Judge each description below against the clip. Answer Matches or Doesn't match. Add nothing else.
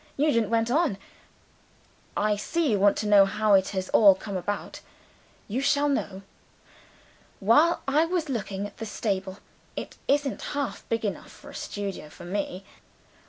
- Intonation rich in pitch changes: Matches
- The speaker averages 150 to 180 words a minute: Matches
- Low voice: Doesn't match